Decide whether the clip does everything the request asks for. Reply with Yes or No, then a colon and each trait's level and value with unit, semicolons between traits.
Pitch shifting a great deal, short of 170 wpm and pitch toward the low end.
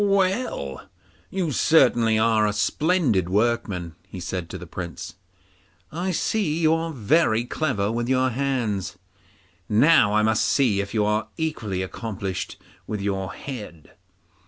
Yes: wide, 7.4 semitones; slow, 135 wpm; low, 110 Hz